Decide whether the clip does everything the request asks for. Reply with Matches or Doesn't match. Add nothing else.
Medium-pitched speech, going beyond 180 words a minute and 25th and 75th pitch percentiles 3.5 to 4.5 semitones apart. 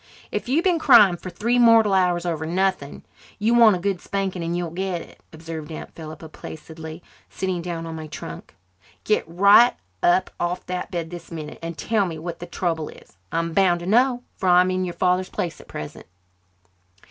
Doesn't match